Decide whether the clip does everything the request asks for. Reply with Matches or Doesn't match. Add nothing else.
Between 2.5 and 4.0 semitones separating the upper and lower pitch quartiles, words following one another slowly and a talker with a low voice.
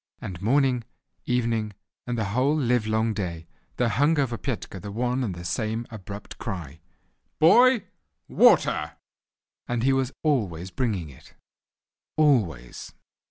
Doesn't match